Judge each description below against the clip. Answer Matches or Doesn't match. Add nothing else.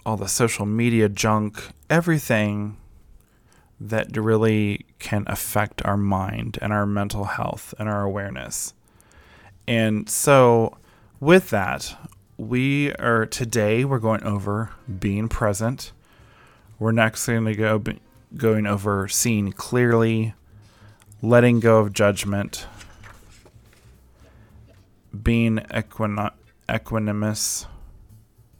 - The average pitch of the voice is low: Matches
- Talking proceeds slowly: Matches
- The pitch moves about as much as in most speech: Doesn't match